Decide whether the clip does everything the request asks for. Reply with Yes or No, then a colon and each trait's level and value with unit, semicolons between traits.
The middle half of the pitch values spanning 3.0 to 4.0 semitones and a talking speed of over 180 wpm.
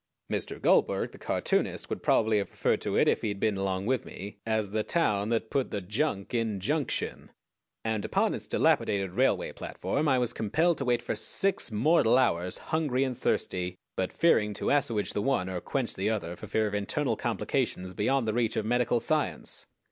No: average, 4.4 semitones; average, 195 wpm